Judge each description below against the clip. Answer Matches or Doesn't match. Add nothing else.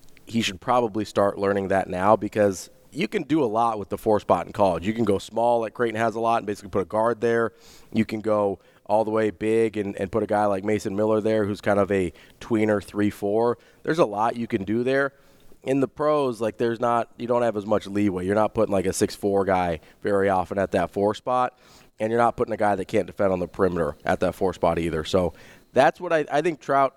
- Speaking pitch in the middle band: Doesn't match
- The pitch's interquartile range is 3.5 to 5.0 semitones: Doesn't match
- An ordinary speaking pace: Doesn't match